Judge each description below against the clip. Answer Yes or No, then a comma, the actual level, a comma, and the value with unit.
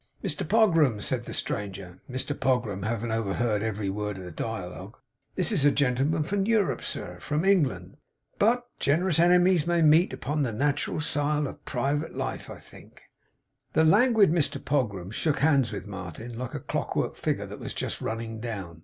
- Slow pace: No, average, 180 wpm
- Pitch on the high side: No, low, 135 Hz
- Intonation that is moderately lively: No, wide, 7.0 semitones